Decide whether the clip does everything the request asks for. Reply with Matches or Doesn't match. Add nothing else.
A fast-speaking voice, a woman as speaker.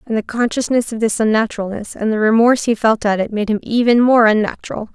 Matches